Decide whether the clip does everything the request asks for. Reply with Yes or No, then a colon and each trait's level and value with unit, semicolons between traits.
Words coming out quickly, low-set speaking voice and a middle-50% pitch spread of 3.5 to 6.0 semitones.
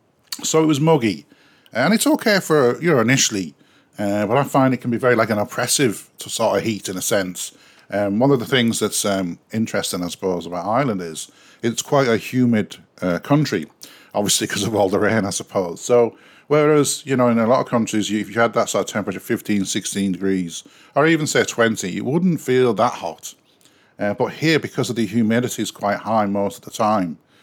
Yes: fast, 215 wpm; low, 115 Hz; average, 4.7 semitones